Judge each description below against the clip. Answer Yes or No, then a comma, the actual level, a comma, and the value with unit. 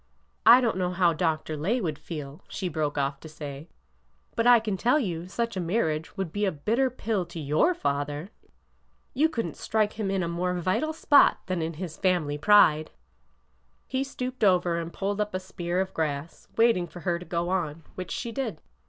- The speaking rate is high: Yes, fast, 210 wpm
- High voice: No, medium, 180 Hz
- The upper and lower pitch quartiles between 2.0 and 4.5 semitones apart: No, average, 5.2 semitones